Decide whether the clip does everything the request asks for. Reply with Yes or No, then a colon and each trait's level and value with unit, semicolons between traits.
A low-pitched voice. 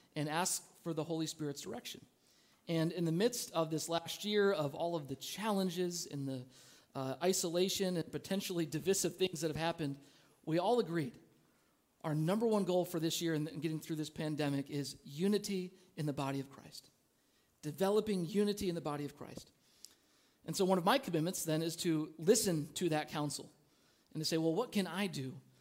No: medium, 165 Hz